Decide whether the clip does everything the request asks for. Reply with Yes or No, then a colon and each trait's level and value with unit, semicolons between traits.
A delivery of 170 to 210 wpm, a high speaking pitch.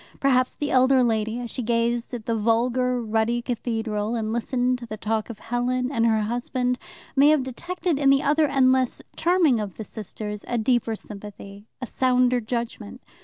Yes: average, 180 wpm; high, 240 Hz